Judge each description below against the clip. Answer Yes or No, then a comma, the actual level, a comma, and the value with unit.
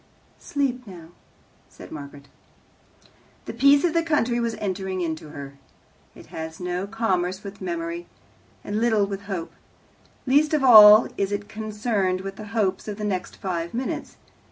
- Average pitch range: Yes, average, 4.3 semitones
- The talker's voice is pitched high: Yes, high, 200 Hz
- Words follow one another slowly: No, average, 155 wpm